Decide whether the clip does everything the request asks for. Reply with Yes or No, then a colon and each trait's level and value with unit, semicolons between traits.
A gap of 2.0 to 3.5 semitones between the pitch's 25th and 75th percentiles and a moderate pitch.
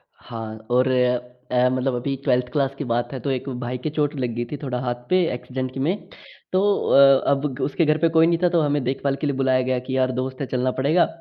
No: narrow, 2.6 semitones; low, 130 Hz